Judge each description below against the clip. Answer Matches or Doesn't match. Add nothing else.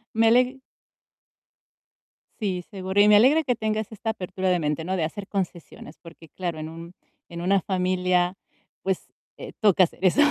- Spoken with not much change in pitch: Doesn't match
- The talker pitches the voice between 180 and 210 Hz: Matches